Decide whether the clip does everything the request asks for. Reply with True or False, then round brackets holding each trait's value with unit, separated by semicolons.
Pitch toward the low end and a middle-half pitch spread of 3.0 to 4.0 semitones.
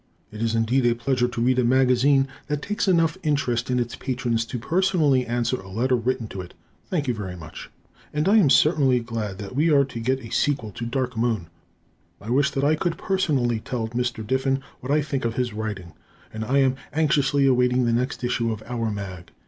True (125 Hz; 3.3 semitones)